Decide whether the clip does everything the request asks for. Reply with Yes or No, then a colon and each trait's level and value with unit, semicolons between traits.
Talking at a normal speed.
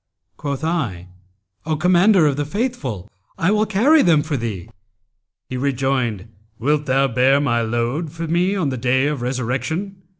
Yes: average, 160 wpm